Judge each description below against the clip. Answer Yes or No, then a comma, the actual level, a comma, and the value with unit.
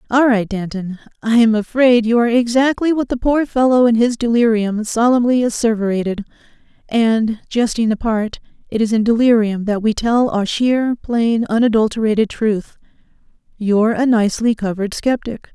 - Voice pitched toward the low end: No, high, 230 Hz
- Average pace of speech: Yes, average, 145 wpm